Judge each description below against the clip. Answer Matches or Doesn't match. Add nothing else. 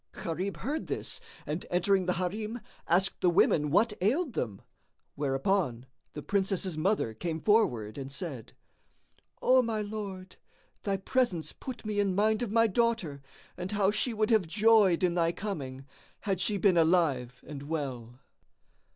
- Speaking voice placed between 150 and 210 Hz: Matches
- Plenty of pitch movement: Matches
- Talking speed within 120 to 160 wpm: Matches